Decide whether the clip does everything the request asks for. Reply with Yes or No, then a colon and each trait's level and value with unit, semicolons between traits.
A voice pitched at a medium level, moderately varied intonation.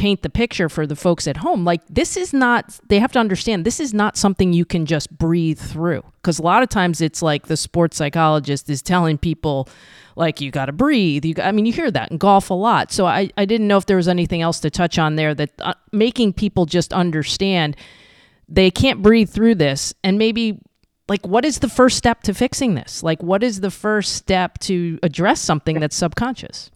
Yes: medium, 180 Hz; average, 4.9 semitones